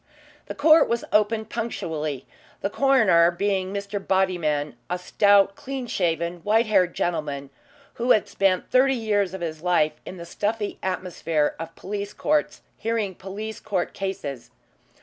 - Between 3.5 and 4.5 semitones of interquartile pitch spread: Yes, average, 4.1 semitones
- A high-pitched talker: Yes, high, 195 Hz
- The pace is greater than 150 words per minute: No, average, 145 wpm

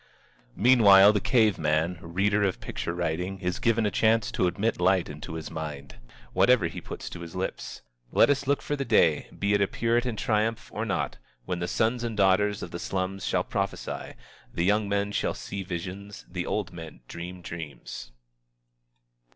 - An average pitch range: Yes, average, 3.7 semitones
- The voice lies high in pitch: No, very low, 95 Hz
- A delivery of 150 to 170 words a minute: No, average, 185 wpm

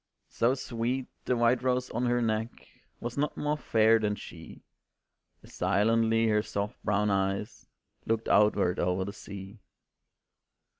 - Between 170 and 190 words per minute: No, average, 140 wpm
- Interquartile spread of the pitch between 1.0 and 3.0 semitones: Yes, average, 2.7 semitones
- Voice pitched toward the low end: Yes, low, 110 Hz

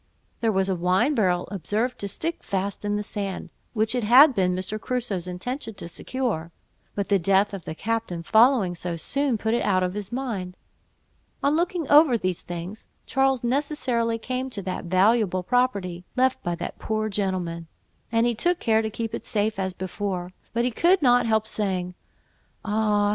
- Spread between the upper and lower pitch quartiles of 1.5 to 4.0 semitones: No, average, 4.8 semitones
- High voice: Yes, high, 210 Hz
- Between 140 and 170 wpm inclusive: No, average, 180 wpm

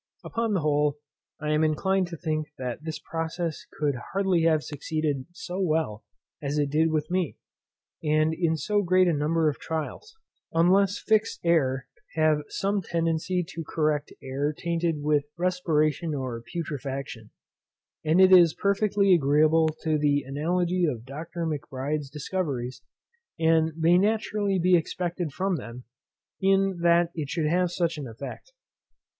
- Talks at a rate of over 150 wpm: No, average, 145 wpm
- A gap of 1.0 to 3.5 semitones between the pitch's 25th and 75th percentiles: Yes, average, 3.2 semitones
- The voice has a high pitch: No, medium, 160 Hz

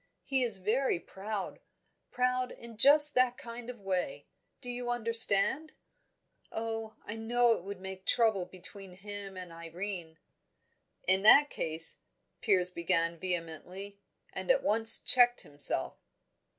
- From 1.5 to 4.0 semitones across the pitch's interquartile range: No, average, 4.6 semitones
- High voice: Yes, high, 210 Hz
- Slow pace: Yes, slow, 130 wpm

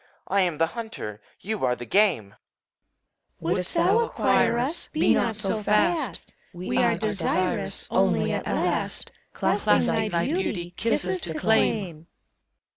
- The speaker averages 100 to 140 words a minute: Yes, slow, 135 wpm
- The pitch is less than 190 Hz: No, high, 200 Hz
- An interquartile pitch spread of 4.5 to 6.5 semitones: Yes, average, 4.9 semitones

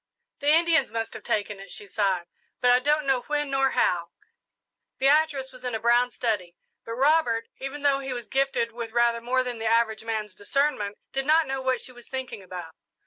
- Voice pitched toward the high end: Yes, high, 245 Hz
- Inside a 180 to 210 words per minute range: Yes, average, 200 wpm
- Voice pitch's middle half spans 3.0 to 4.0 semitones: Yes, average, 3.5 semitones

